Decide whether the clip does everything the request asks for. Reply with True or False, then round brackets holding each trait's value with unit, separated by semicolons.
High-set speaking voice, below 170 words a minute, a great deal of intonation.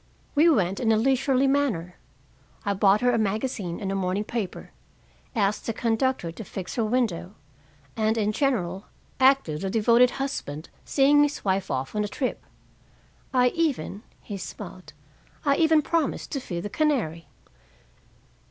True (220 Hz; 150 wpm; 5.7 semitones)